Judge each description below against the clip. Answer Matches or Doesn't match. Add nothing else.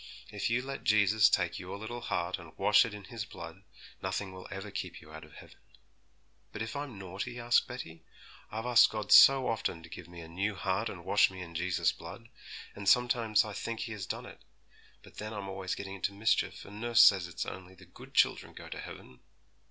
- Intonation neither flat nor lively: Matches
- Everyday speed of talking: Doesn't match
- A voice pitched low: Matches